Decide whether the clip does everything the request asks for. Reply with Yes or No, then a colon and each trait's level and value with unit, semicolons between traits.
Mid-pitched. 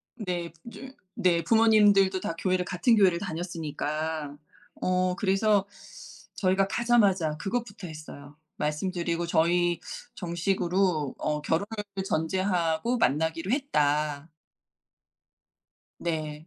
Yes: medium, 175 Hz